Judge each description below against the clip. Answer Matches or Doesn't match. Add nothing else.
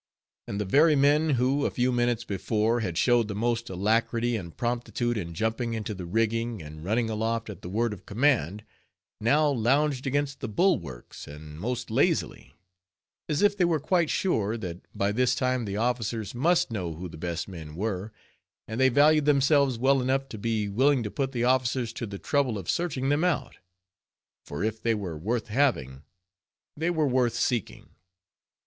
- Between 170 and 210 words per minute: Matches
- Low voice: Matches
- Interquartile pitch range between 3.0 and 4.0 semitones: Doesn't match